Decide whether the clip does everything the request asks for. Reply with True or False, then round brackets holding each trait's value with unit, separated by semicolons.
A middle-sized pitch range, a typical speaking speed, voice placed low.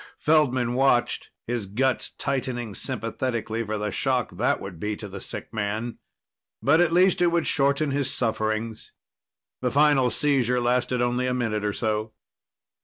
True (3.8 semitones; 155 wpm; 120 Hz)